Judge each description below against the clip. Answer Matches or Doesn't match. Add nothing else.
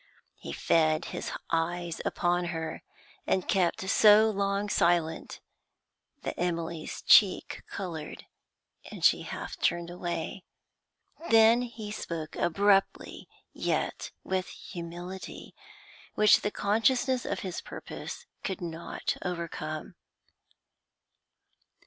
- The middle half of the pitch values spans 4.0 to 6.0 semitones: Doesn't match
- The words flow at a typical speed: Doesn't match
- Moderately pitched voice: Matches